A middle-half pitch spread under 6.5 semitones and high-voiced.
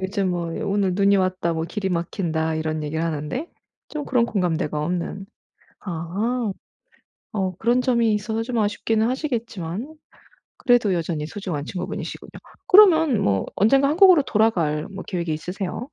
Yes: wide, 5.6 semitones; high, 195 Hz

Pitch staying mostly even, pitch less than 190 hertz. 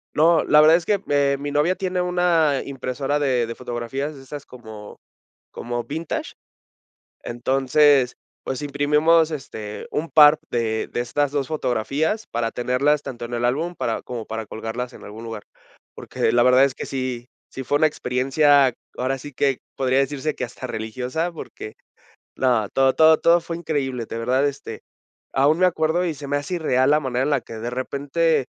No: average, 3.6 semitones; low, 135 Hz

